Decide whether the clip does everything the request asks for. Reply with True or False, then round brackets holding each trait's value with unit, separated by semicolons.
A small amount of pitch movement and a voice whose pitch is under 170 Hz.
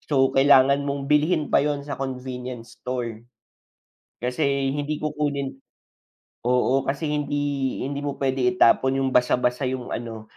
True (2.3 semitones; 135 Hz)